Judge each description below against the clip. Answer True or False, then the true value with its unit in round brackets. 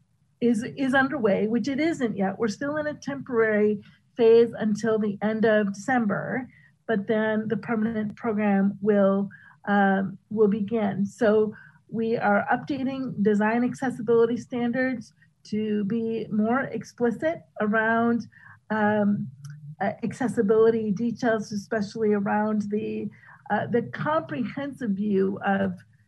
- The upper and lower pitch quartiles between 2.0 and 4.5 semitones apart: True (2.5 semitones)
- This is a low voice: False (215 Hz)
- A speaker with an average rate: False (115 wpm)